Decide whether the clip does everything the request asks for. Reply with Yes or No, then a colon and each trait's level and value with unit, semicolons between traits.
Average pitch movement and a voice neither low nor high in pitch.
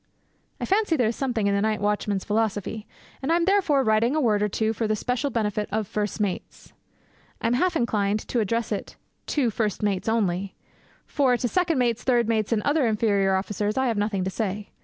No: average, 3.2 semitones; high, 220 Hz